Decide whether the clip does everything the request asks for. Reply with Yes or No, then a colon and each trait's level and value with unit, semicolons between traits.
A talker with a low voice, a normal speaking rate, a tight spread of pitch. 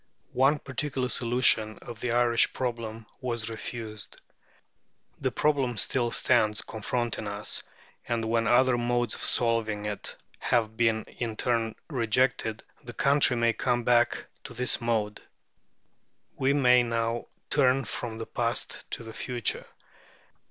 No: low, 120 Hz; slow, 130 wpm; narrow, 1.9 semitones